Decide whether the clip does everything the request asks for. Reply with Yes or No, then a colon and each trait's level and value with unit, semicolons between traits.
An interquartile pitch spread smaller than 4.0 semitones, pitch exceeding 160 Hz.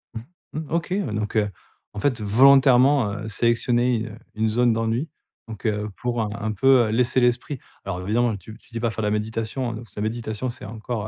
No: narrow, 2.4 semitones; low, 115 Hz